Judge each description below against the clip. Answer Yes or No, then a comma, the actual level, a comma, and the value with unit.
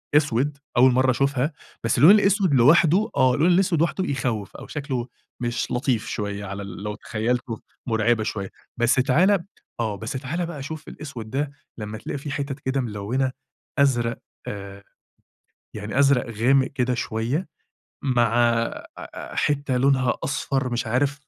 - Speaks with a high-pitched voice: No, low, 130 Hz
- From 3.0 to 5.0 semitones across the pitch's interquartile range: Yes, average, 3.7 semitones